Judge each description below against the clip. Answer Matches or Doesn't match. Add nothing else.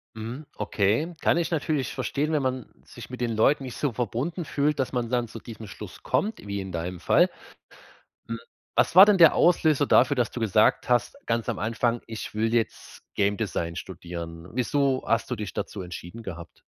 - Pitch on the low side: Matches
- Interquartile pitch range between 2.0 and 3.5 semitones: Doesn't match